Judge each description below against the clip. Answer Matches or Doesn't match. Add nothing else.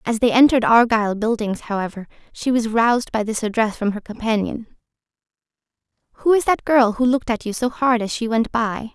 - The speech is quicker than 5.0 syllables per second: Matches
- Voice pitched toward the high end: Matches